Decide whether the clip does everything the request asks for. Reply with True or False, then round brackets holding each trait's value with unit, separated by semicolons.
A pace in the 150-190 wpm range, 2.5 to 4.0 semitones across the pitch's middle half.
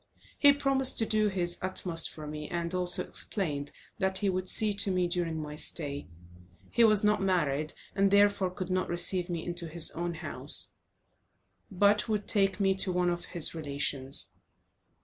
True (170 wpm; 3.4 semitones)